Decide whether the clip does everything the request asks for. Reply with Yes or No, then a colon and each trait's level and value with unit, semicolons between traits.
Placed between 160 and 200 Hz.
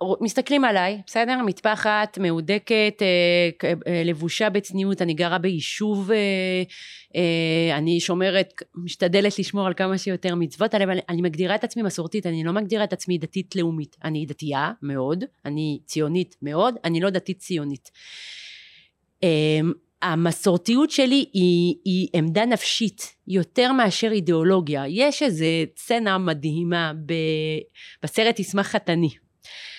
Yes: medium, 185 Hz